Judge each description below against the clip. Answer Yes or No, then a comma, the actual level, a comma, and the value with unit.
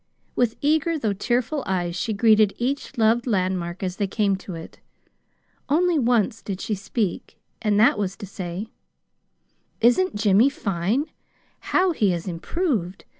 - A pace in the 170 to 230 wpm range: No, average, 145 wpm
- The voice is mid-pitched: No, high, 210 Hz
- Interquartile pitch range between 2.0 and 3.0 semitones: No, average, 4.6 semitones